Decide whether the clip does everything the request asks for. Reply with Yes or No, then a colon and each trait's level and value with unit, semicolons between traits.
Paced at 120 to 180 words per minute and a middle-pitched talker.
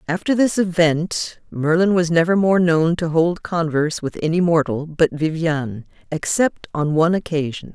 Yes: average, 155 wpm; medium, 165 Hz